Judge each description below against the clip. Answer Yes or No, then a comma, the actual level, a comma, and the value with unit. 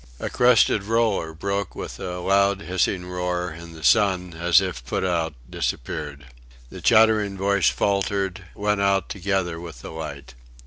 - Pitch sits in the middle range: No, very low, 95 Hz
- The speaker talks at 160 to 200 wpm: No, average, 150 wpm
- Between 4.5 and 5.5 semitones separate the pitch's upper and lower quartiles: No, average, 3.1 semitones